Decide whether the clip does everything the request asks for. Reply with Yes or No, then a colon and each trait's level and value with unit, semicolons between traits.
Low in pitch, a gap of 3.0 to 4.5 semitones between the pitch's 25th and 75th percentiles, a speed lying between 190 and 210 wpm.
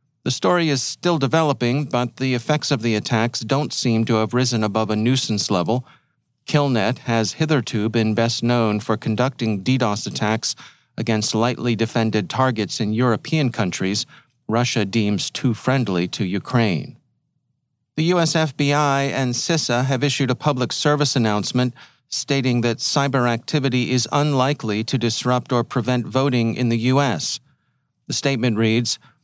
No: low, 125 Hz; average, 3.4 semitones; average, 145 wpm